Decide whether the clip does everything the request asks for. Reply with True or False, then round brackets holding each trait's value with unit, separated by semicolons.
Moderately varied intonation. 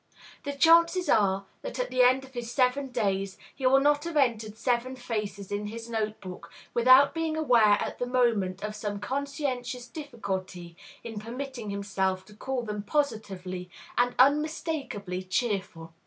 True (4.9 semitones)